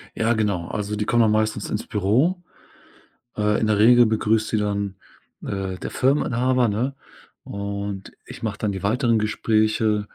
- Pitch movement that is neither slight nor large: No, narrow, 2.2 semitones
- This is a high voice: No, low, 110 Hz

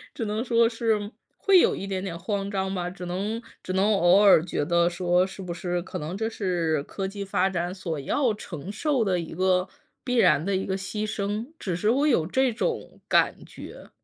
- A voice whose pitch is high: Yes, high, 195 Hz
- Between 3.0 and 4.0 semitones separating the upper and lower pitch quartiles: Yes, average, 3.3 semitones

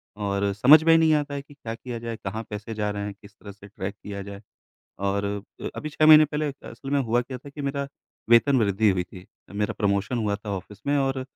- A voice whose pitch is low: Yes, low, 115 Hz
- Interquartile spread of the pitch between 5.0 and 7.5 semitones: Yes, wide, 5.6 semitones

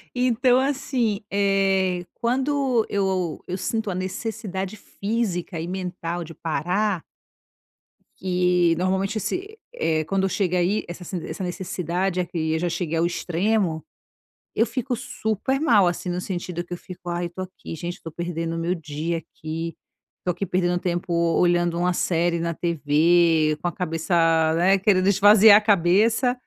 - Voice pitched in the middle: Yes, medium, 180 Hz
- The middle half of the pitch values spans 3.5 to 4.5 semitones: No, average, 3.0 semitones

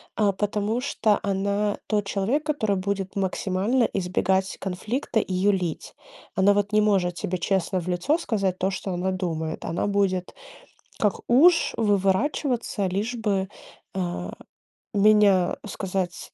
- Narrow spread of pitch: Yes, narrow, 2.2 semitones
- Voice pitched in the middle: No, high, 195 Hz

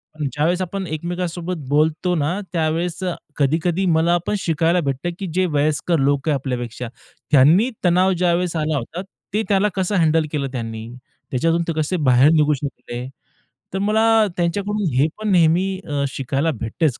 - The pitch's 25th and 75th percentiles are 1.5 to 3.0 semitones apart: No, average, 4.1 semitones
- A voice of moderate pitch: Yes, medium, 165 Hz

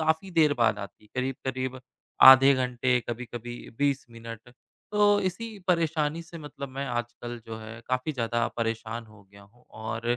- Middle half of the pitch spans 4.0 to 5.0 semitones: Yes, average, 4.3 semitones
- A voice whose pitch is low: Yes, low, 125 Hz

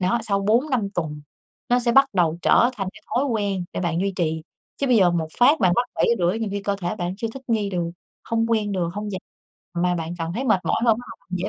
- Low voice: No, high, 200 Hz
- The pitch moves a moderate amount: Yes, average, 4.7 semitones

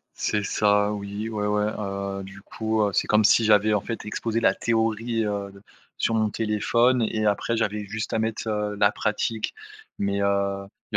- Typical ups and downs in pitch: No, narrow, 1.6 semitones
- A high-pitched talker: No, low, 105 Hz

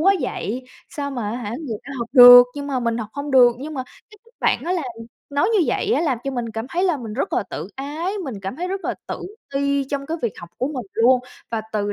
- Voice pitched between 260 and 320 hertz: Yes, very high, 265 Hz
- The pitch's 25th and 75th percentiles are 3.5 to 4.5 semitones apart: Yes, average, 3.8 semitones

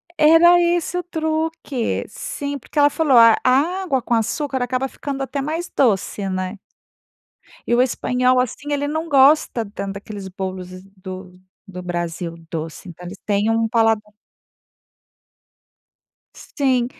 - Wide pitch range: Yes, wide, 6.7 semitones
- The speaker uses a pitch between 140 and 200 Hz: No, very high, 250 Hz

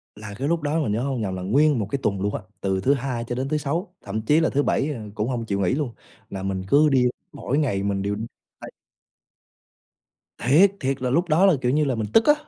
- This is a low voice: Yes, low, 130 Hz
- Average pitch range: No, wide, 6.1 semitones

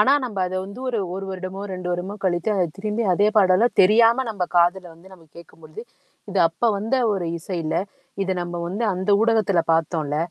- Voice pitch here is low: No, high, 190 Hz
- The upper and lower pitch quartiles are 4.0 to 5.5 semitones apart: No, average, 3.2 semitones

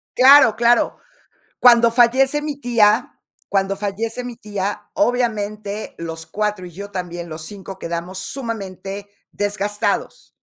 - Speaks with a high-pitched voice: Yes, high, 205 Hz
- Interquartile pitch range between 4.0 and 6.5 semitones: No, average, 3.6 semitones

